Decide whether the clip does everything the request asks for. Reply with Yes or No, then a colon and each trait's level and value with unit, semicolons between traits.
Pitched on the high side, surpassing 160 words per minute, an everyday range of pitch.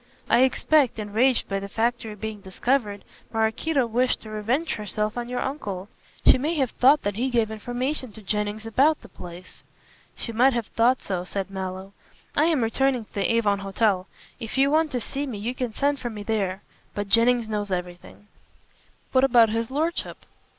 Yes: high, 225 Hz; average, 185 wpm; average, 4.0 semitones